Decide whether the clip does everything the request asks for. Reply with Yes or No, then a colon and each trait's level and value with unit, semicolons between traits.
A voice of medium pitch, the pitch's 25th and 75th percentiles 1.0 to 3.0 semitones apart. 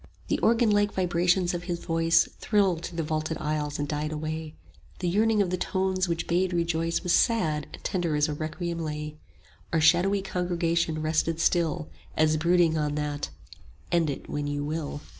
Yes: medium, 165 Hz; narrow, 2.6 semitones